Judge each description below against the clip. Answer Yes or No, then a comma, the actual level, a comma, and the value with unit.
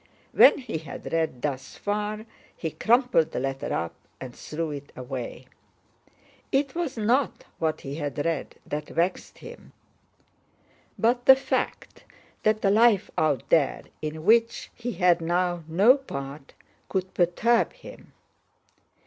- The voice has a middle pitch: Yes, medium, 175 Hz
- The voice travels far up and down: Yes, wide, 7.5 semitones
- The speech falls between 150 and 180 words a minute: No, slow, 135 wpm